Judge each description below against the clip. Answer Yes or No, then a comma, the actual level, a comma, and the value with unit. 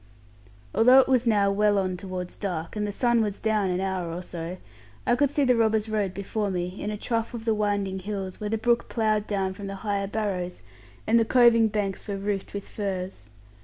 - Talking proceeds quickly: Yes, fast, 215 wpm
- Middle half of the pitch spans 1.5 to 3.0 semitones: Yes, narrow, 2.6 semitones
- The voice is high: Yes, high, 205 Hz